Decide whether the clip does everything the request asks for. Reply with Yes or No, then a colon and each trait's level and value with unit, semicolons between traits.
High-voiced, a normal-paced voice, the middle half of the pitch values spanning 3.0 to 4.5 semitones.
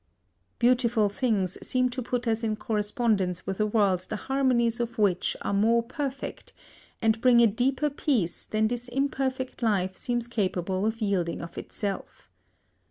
Yes: high, 225 Hz; average, 155 wpm; average, 3.5 semitones